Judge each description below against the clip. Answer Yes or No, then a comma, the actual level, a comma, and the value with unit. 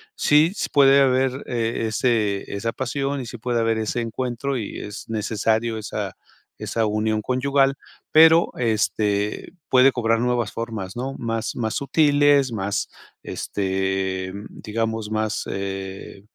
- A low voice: Yes, low, 115 Hz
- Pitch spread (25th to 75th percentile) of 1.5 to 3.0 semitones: No, average, 3.6 semitones